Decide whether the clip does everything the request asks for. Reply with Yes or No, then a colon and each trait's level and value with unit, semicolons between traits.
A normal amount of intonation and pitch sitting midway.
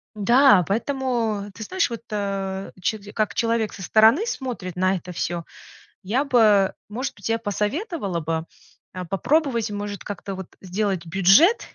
No: average, 3.8 semitones; high, 205 Hz